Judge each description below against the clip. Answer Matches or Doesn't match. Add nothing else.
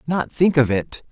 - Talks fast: Matches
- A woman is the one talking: Doesn't match